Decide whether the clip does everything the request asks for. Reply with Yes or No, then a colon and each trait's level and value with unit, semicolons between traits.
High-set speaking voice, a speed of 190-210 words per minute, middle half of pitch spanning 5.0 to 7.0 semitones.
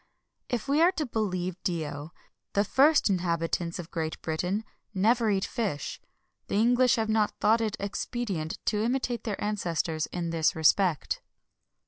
No: high, 200 Hz; average, 150 wpm; wide, 5.4 semitones